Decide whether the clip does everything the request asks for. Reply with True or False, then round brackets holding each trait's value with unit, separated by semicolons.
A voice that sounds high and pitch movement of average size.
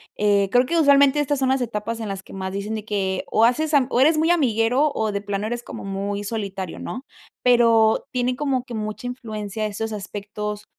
True (220 Hz; 3.7 semitones)